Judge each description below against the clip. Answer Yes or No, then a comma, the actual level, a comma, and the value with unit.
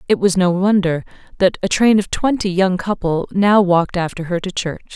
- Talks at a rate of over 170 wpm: Yes, fast, 205 wpm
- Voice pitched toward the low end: No, medium, 185 Hz